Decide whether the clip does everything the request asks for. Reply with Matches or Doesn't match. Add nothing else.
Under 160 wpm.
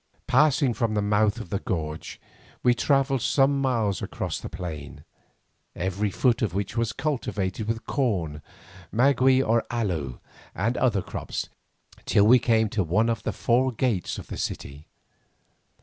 Matches